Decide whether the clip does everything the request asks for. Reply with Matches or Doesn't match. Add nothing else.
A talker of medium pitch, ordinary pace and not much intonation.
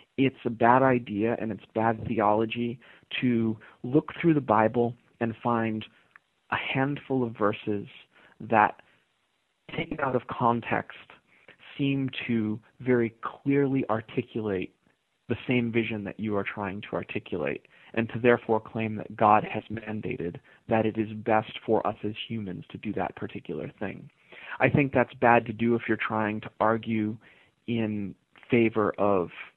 Doesn't match